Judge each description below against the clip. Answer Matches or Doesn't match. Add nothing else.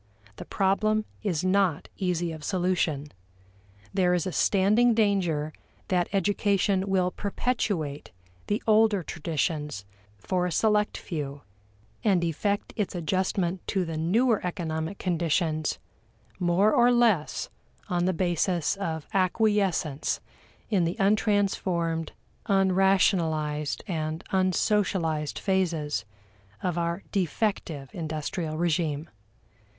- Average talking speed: Doesn't match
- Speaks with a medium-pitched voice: Matches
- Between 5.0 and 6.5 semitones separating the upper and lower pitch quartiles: Doesn't match